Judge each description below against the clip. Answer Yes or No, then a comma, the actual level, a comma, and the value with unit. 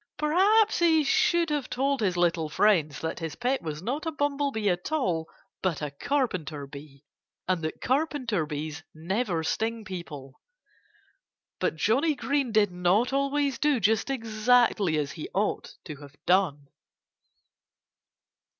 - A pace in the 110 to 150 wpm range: Yes, average, 140 wpm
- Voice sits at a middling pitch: No, high, 210 Hz